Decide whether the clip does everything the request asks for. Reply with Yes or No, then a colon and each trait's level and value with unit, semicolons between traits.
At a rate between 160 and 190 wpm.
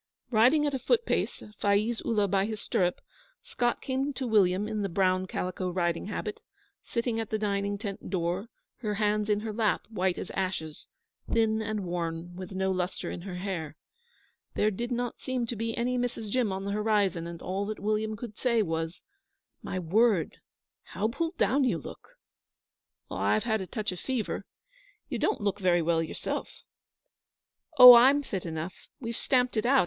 Yes: average, 180 wpm